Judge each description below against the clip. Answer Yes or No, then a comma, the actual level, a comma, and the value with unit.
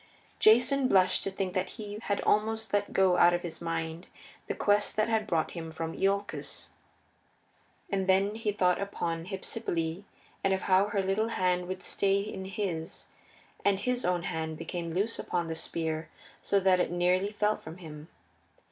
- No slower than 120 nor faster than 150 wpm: No, average, 175 wpm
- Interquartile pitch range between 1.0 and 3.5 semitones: Yes, average, 3.1 semitones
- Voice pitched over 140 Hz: Yes, high, 190 Hz